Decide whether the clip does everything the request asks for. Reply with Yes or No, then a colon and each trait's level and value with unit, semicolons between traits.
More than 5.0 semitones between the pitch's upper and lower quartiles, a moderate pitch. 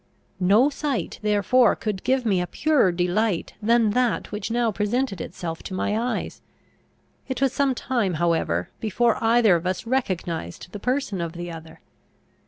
No: wide, 5.4 semitones; high, 210 Hz